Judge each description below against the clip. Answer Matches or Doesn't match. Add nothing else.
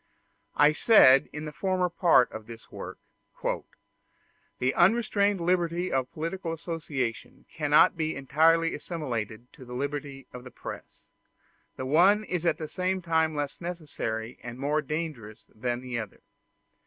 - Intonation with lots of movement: Doesn't match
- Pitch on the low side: Doesn't match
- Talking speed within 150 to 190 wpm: Doesn't match